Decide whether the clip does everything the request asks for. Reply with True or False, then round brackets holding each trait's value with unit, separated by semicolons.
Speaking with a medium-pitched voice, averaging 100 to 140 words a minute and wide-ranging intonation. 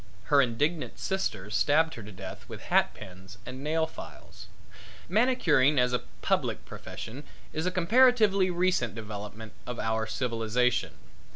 False (130 Hz; 135 wpm; 7.6 semitones)